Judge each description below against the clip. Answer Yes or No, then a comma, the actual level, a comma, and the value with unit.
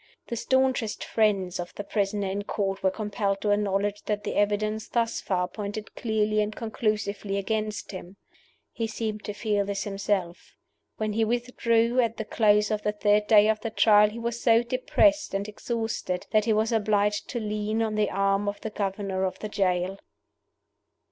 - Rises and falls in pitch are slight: Yes, narrow, 1.7 semitones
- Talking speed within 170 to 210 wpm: Yes, average, 180 wpm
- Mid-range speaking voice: No, high, 210 Hz